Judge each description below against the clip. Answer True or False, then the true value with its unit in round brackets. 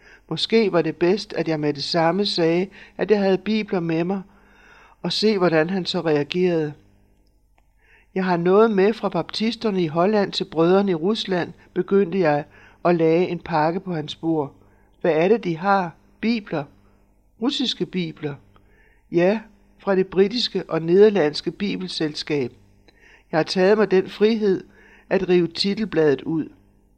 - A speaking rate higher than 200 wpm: False (150 wpm)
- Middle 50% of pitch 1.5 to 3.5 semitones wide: False (4.0 semitones)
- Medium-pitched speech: True (180 Hz)